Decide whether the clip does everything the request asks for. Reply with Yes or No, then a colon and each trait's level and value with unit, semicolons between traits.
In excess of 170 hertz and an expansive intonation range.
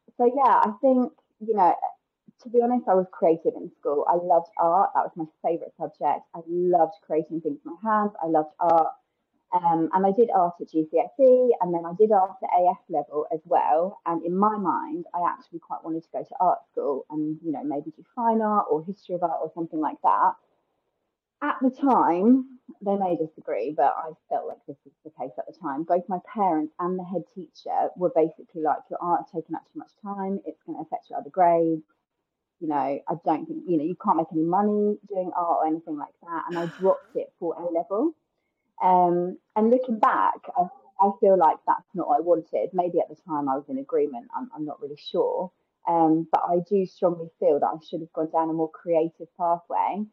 Yes: high, 190 Hz; wide, 8.1 semitones